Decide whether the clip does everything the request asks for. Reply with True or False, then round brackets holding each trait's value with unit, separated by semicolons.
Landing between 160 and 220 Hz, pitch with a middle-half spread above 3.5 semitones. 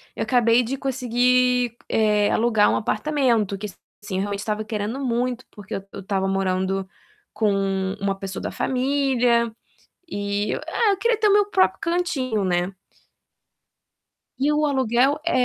False (230 Hz; 4.1 semitones)